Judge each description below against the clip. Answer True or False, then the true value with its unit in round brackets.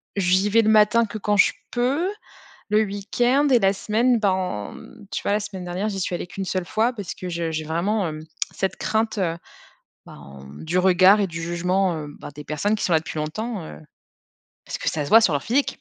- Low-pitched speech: False (195 Hz)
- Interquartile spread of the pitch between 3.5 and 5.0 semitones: True (4.1 semitones)